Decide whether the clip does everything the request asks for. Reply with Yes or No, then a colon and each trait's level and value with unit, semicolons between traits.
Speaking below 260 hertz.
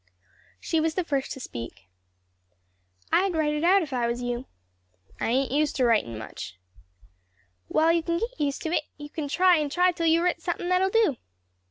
No: very high, 310 Hz